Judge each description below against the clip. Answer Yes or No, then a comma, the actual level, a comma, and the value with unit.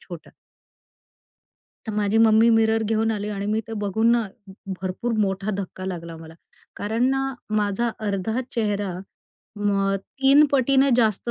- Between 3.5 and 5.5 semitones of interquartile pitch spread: No, average, 2.7 semitones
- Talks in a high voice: Yes, high, 215 Hz